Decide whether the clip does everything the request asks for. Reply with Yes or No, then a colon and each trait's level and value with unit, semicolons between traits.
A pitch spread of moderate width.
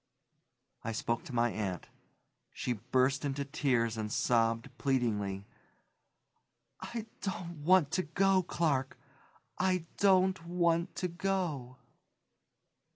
No: wide, 7.4 semitones